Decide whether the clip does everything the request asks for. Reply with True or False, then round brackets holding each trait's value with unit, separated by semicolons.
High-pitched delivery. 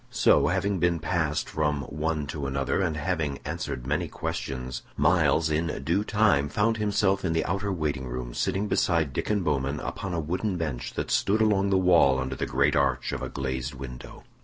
False (80 Hz)